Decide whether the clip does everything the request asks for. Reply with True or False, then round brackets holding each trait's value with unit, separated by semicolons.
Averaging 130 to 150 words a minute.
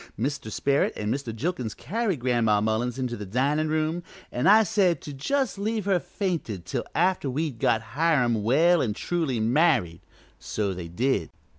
False (165 wpm)